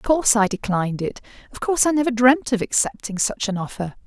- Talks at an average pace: No, fast, 220 wpm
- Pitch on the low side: No, high, 230 Hz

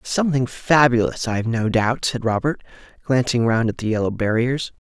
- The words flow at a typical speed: Yes, average, 170 wpm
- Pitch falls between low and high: No, low, 120 Hz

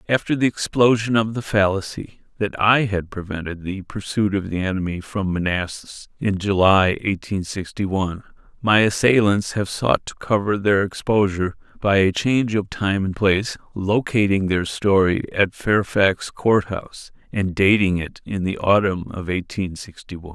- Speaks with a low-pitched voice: Yes, low, 100 Hz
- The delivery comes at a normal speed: Yes, average, 160 wpm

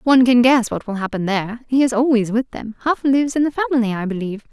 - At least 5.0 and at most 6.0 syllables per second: No, 6.9 syllables/s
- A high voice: Yes, high, 240 Hz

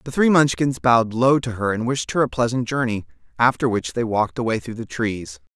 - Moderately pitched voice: No, low, 120 Hz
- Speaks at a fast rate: Yes, fast, 225 wpm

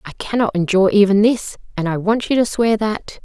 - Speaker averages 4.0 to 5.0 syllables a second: No, 5.7 syllables/s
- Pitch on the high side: Yes, high, 210 Hz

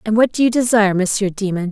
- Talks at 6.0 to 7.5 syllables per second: Yes, 6.8 syllables/s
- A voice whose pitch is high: Yes, high, 210 Hz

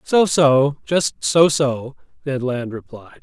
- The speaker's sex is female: No, male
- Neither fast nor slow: Yes, average, 150 wpm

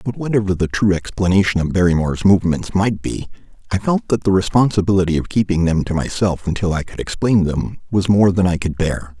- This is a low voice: Yes, very low, 95 Hz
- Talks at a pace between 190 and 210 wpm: Yes, average, 200 wpm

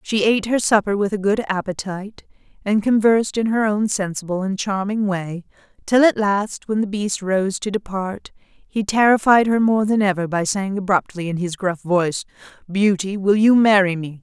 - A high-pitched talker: Yes, high, 200 Hz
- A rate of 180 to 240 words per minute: Yes, average, 185 wpm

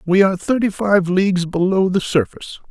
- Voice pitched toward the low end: No, high, 190 Hz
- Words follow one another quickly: No, average, 180 wpm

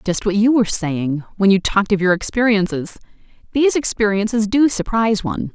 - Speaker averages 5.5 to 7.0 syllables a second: Yes, 5.9 syllables/s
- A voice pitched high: Yes, high, 210 Hz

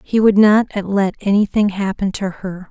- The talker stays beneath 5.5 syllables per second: Yes, 4.5 syllables/s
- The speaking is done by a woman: Yes, female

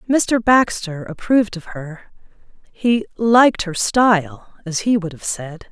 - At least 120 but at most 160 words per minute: Yes, average, 145 wpm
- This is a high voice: Yes, high, 200 Hz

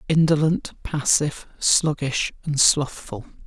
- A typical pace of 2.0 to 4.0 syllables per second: Yes, 3.9 syllables/s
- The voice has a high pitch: No, medium, 145 Hz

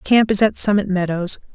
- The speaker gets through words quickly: No, average, 195 wpm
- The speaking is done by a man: No, female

